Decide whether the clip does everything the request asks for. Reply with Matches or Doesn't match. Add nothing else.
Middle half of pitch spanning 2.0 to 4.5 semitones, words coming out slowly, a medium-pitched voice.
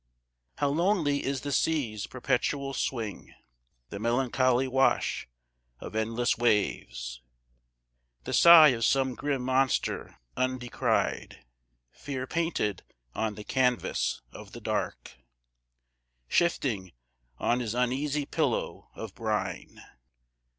Doesn't match